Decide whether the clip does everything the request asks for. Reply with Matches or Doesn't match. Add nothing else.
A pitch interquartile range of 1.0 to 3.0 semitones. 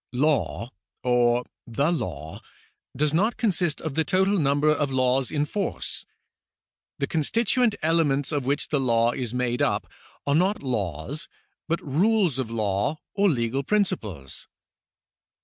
Doesn't match